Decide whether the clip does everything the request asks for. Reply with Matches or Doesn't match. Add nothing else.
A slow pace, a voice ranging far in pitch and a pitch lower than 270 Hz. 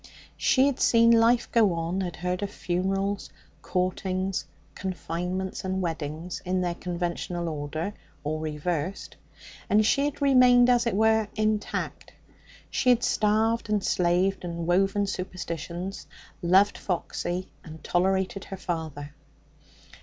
Doesn't match